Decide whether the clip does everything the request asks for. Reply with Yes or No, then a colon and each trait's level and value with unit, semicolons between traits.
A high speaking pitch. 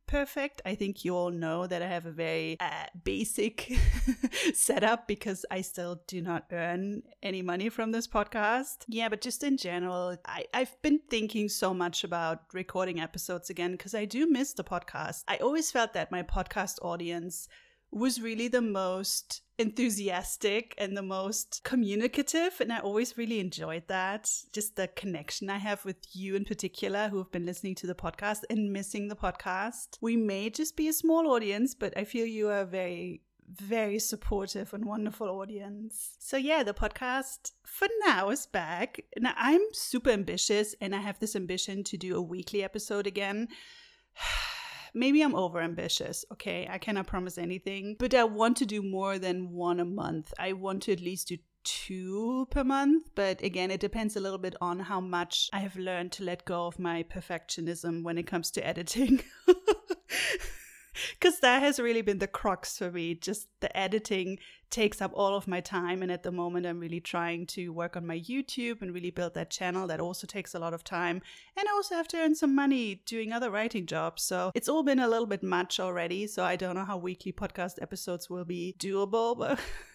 Yes: high, 200 Hz